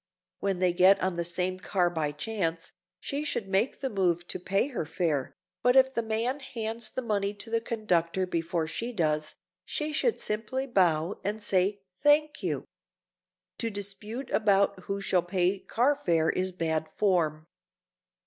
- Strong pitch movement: No, average, 4.7 semitones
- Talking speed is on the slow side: No, average, 165 wpm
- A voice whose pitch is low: No, high, 195 Hz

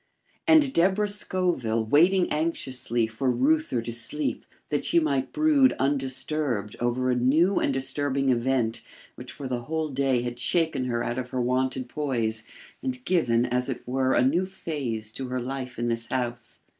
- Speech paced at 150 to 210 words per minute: Yes, average, 170 wpm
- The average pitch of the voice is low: Yes, low, 130 Hz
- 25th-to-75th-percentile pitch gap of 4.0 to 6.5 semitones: Yes, average, 4.6 semitones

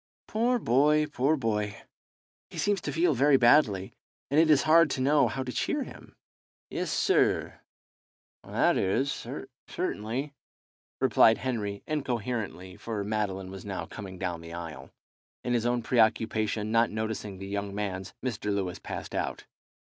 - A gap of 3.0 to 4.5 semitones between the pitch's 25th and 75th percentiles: No, average, 5.2 semitones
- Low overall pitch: Yes, low, 110 Hz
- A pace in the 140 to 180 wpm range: Yes, average, 145 wpm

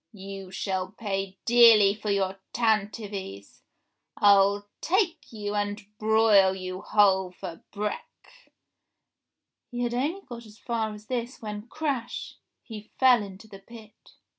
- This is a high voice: Yes, high, 210 Hz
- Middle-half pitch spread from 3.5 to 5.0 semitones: No, average, 3.0 semitones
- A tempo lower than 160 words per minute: Yes, average, 140 wpm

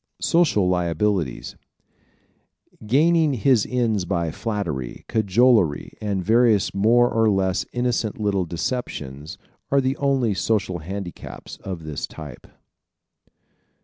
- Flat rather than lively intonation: No, wide, 5.6 semitones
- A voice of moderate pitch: No, low, 105 Hz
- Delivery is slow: Yes, slow, 110 wpm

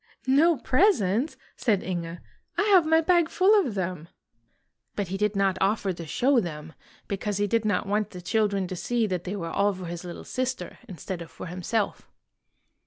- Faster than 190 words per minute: Yes, average, 200 wpm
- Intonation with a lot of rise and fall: Yes, wide, 5.7 semitones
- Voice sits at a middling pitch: No, high, 205 Hz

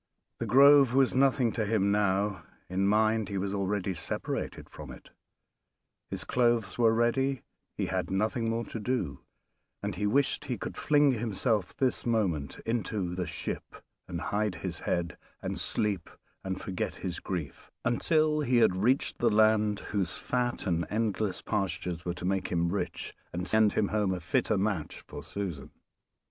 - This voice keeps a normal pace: Yes, average, 160 wpm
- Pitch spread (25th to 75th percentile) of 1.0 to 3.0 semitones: No, average, 4.0 semitones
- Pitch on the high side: No, low, 105 Hz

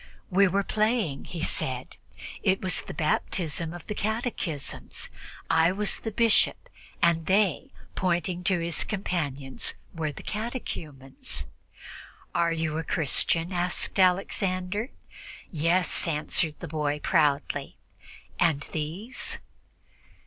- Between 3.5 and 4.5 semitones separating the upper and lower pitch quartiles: Yes, average, 4.0 semitones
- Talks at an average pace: No, slow, 110 wpm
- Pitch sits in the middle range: Yes, medium, 175 Hz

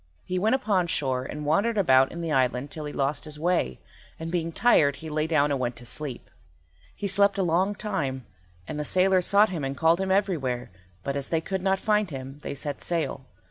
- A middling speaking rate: No, fast, 220 wpm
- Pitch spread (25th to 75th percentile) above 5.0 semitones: Yes, wide, 5.5 semitones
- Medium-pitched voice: Yes, medium, 160 Hz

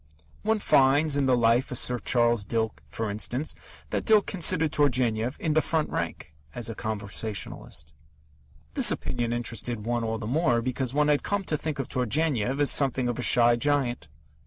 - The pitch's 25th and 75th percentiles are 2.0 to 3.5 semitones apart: No, average, 4.0 semitones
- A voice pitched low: Yes, low, 125 Hz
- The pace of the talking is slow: No, average, 180 wpm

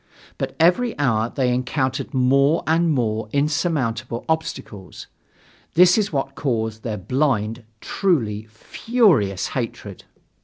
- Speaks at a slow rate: Yes, slow, 110 wpm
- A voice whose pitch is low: Yes, low, 130 Hz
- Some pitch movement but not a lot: No, wide, 6.2 semitones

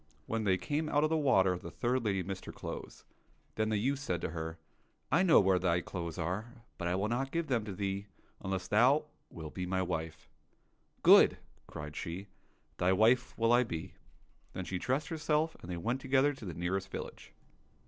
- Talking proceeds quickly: Yes, fast, 215 wpm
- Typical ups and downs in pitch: No, wide, 6.4 semitones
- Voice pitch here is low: Yes, low, 100 Hz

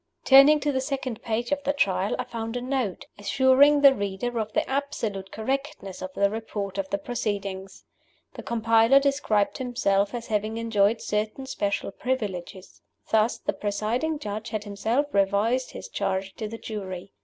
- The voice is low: No, high, 220 Hz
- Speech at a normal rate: Yes, average, 165 wpm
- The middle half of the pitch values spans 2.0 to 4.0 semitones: No, average, 4.5 semitones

